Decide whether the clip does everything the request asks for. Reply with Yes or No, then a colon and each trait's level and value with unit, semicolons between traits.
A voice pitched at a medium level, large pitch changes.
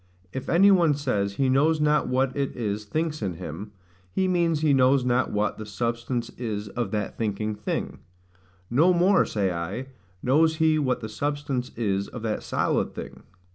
No: low, 125 Hz; wide, 6.0 semitones